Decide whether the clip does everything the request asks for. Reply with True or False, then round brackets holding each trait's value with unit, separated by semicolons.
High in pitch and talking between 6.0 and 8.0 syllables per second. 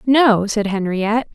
False (220 Hz; 4.2 syllables/s)